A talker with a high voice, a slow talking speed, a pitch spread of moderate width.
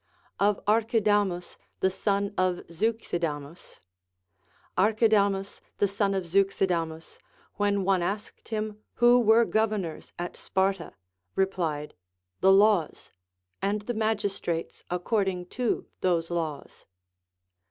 Yes: high, 195 Hz; slow, 100 wpm; average, 3.3 semitones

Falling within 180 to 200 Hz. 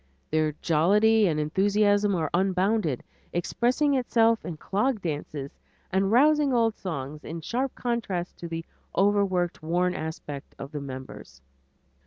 Yes: medium, 185 Hz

